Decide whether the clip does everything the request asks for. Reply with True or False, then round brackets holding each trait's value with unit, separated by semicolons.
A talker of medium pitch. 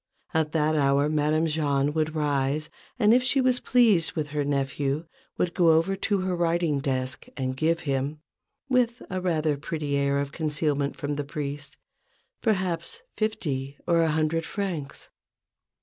True (155 Hz)